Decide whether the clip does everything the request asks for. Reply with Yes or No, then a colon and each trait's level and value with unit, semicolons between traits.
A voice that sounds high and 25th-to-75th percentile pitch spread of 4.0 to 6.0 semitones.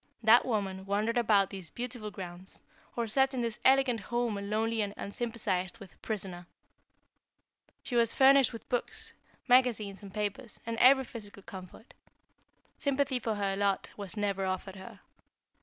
No: high, 215 Hz; average, 3.4 semitones